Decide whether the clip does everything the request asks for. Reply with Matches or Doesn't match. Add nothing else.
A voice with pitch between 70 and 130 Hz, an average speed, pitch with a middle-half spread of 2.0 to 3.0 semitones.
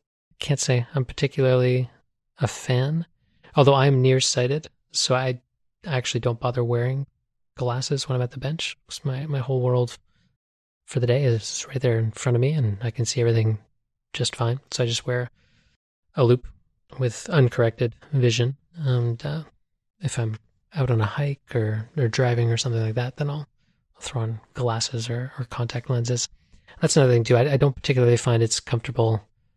Matches